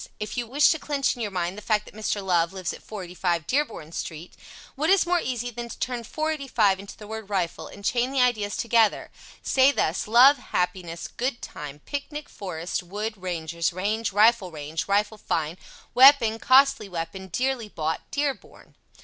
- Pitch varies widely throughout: Yes, wide, 5.7 semitones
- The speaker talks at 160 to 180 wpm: Yes, average, 175 wpm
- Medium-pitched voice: No, high, 210 Hz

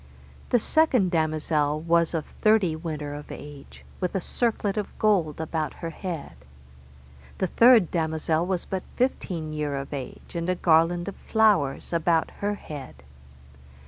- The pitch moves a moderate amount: Yes, average, 3.9 semitones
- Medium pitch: Yes, medium, 165 Hz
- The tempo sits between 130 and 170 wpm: Yes, average, 145 wpm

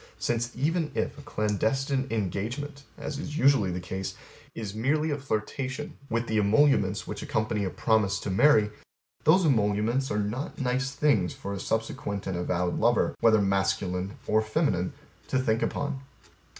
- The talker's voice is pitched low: Yes, low, 110 Hz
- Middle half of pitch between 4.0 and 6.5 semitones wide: Yes, average, 5.3 semitones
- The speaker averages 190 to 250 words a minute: No, average, 155 wpm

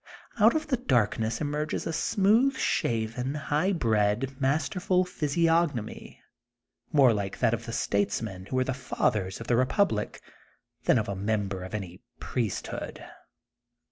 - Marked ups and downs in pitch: Yes, wide, 7.5 semitones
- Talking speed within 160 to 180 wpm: No, average, 140 wpm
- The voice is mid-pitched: No, low, 130 Hz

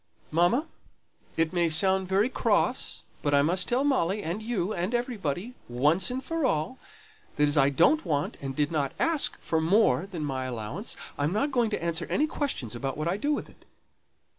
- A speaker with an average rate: Yes, average, 185 wpm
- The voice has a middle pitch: Yes, medium, 175 Hz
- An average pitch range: No, wide, 7.2 semitones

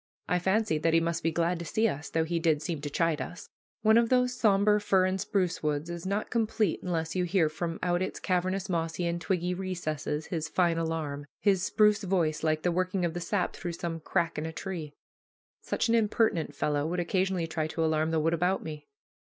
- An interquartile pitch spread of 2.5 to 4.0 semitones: Yes, average, 2.9 semitones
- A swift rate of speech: Yes, fast, 215 wpm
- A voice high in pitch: No, medium, 170 Hz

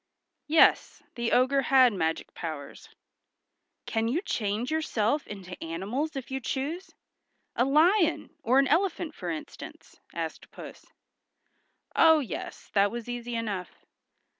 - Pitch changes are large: Yes, wide, 6.6 semitones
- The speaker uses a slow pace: Yes, slow, 125 wpm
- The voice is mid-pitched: No, high, 245 Hz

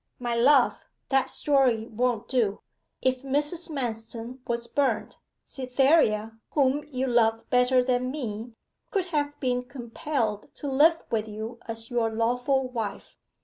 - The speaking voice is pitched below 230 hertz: No, very high, 250 Hz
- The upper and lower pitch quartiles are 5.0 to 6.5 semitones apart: No, average, 3.2 semitones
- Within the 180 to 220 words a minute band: No, slow, 135 wpm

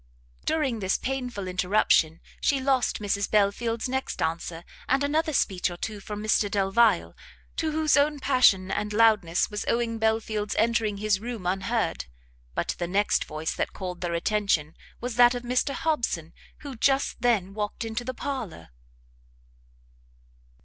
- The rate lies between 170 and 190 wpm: No, average, 150 wpm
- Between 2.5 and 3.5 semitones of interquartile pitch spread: No, average, 4.4 semitones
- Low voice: No, high, 215 Hz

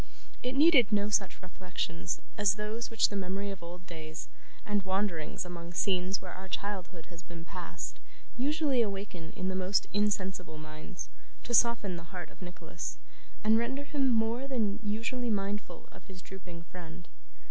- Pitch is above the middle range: Yes, high, 195 Hz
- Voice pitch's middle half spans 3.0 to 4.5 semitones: Yes, average, 3.7 semitones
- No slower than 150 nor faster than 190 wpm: Yes, average, 160 wpm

